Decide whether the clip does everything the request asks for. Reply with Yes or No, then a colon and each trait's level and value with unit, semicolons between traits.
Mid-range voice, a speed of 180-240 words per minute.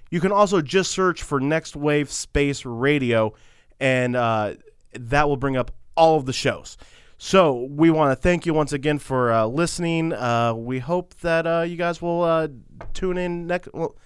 Yes: medium, 150 Hz; average, 190 wpm